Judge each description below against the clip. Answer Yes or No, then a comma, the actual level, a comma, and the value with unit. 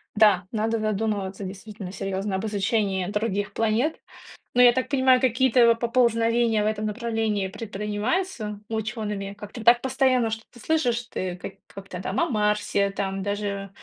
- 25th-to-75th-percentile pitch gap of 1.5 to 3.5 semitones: Yes, average, 2.8 semitones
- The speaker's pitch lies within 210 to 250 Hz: Yes, high, 215 Hz